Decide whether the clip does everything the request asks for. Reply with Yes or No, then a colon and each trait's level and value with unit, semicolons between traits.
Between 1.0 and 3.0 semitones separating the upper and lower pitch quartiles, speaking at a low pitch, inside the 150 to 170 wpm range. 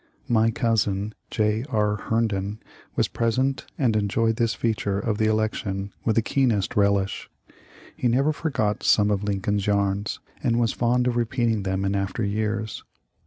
Yes: narrow, 2.4 semitones; low, 110 Hz; average, 155 wpm